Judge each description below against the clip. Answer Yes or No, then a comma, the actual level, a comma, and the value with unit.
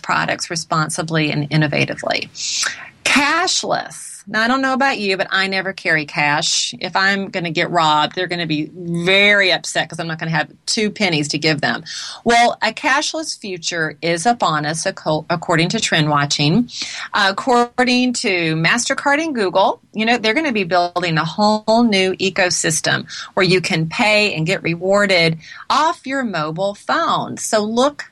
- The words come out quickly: No, average, 165 wpm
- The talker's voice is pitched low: No, high, 190 Hz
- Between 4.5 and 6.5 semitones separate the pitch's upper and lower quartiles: Yes, wide, 5.5 semitones